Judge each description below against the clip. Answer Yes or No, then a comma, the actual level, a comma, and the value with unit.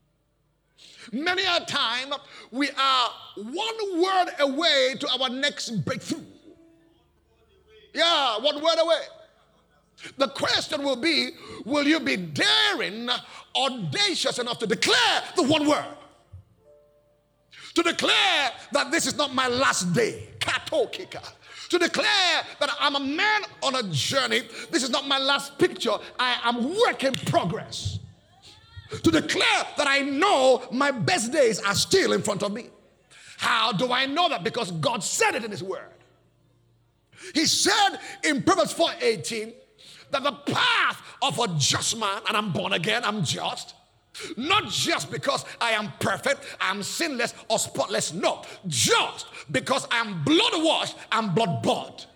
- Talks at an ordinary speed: Yes, average, 145 wpm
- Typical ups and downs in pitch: No, wide, 6.2 semitones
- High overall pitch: Yes, very high, 280 Hz